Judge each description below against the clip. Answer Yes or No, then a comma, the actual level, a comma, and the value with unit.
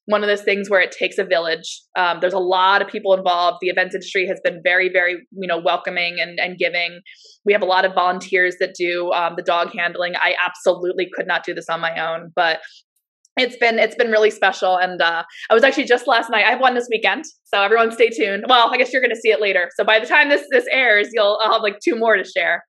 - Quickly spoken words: Yes, fast, 260 wpm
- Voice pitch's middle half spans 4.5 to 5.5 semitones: No, average, 3.7 semitones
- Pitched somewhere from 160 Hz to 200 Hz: Yes, medium, 185 Hz